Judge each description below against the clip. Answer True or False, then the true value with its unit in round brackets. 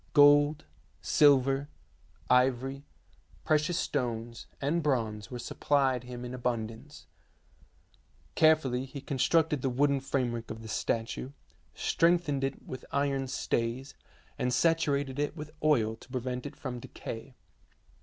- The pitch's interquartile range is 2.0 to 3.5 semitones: True (2.8 semitones)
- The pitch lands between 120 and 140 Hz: True (135 Hz)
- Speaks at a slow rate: True (120 wpm)